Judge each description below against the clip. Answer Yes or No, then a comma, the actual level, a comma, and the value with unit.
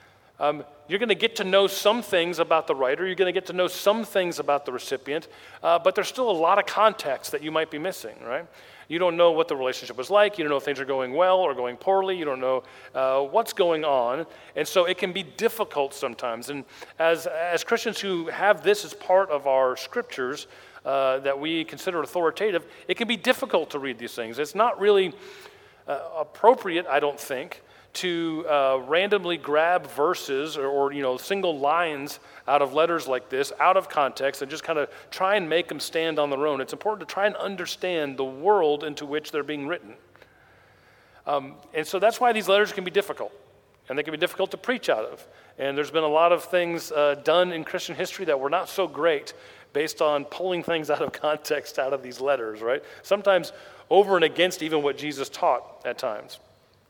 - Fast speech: Yes, fast, 215 wpm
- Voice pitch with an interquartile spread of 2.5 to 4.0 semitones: No, average, 5.2 semitones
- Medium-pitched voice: Yes, medium, 165 Hz